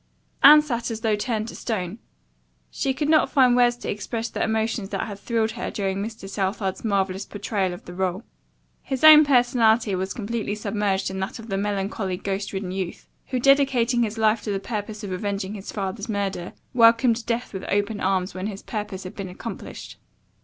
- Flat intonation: No, average, 3.2 semitones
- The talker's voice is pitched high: Yes, high, 210 Hz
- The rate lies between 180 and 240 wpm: Yes, average, 190 wpm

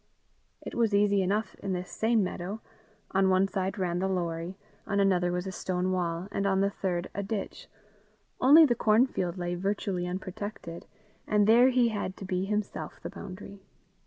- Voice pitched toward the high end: Yes, high, 195 Hz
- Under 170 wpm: No, average, 175 wpm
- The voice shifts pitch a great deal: No, narrow, 2.4 semitones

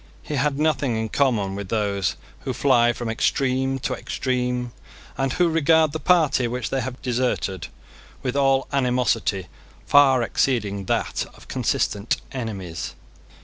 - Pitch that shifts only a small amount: No, average, 3.5 semitones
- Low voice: Yes, low, 125 Hz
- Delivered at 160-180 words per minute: No, average, 140 wpm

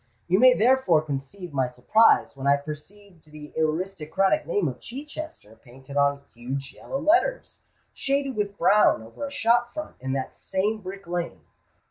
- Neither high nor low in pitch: Yes, medium, 180 Hz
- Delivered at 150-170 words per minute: Yes, average, 155 wpm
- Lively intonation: Yes, wide, 8.2 semitones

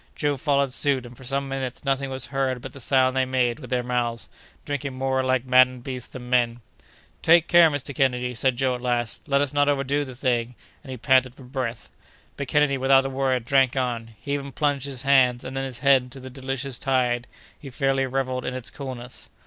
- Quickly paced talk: Yes, fast, 215 wpm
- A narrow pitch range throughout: Yes, narrow, 1.6 semitones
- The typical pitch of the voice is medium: No, low, 130 Hz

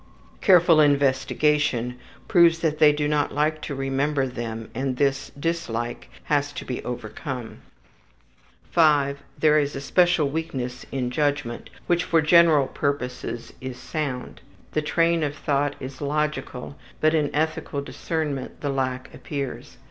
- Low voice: No, medium, 145 Hz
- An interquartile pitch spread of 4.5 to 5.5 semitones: No, average, 2.8 semitones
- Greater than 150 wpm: No, slow, 135 wpm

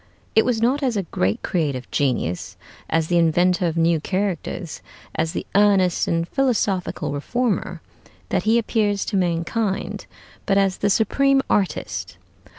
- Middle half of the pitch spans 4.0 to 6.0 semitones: Yes, average, 4.8 semitones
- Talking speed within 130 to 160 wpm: Yes, average, 145 wpm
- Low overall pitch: No, high, 190 Hz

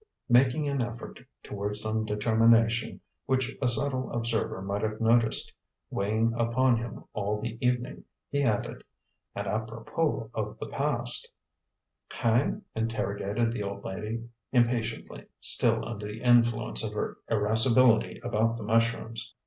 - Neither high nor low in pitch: No, low, 115 Hz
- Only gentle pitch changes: Yes, narrow, 1.9 semitones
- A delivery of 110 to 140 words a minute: Yes, slow, 135 wpm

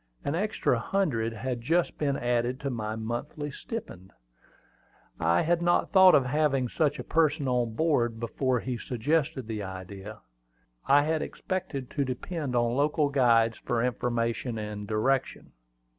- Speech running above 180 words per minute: No, average, 145 wpm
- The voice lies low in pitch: Yes, low, 125 Hz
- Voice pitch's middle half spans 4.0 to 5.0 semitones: Yes, average, 4.4 semitones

